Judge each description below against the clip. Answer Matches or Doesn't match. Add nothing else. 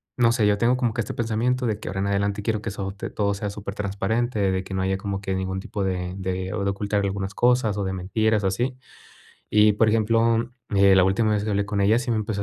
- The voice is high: Doesn't match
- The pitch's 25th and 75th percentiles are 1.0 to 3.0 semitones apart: Matches